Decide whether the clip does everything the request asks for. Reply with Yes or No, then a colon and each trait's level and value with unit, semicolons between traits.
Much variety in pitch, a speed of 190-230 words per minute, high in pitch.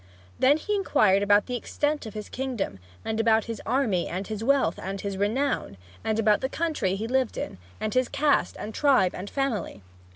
No: average, 4.9 semitones; average, 195 wpm; high, 225 Hz